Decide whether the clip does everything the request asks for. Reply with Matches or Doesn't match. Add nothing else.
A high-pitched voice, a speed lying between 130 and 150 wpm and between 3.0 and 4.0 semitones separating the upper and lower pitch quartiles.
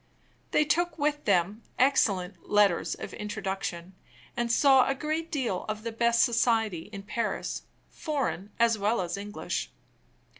Doesn't match